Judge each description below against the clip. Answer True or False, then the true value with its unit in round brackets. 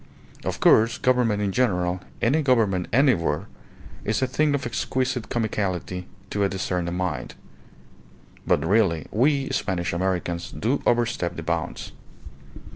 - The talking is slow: True (125 wpm)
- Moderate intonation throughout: False (5.7 semitones)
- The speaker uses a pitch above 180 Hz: False (105 Hz)